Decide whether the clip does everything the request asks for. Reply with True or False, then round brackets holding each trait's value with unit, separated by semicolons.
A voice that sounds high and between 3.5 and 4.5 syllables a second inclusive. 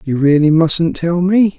False (165 Hz; 4.0 syllables/s)